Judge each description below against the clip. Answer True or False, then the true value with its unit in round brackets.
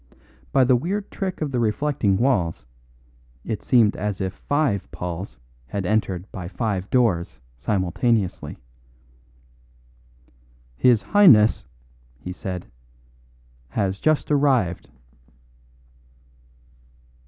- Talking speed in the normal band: False (95 wpm)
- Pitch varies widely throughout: True (5.9 semitones)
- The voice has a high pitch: False (105 Hz)